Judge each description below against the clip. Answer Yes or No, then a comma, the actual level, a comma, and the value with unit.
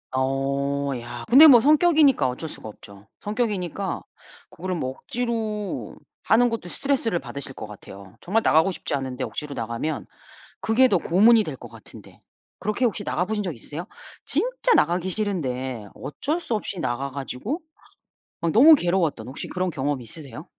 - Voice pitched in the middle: Yes, medium, 175 Hz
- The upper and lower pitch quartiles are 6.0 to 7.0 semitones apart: No, wide, 8.9 semitones